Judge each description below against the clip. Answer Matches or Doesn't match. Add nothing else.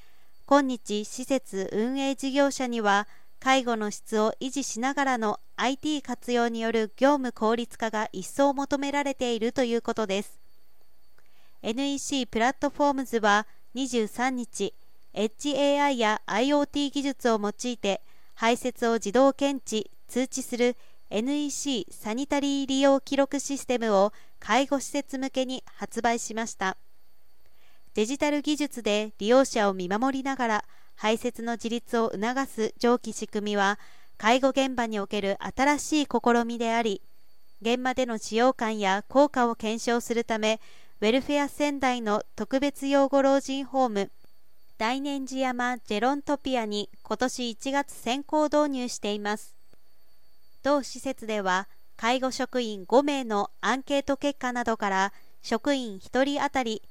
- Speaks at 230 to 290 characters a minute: Matches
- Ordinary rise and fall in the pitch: Matches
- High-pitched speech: Matches